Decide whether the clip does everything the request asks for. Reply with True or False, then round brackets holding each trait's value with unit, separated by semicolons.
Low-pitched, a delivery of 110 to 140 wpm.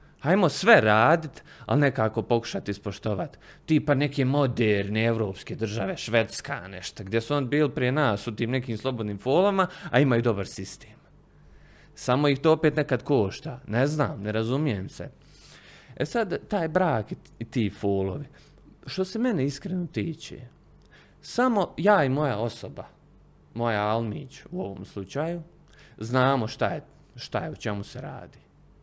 False (125 Hz; 150 wpm)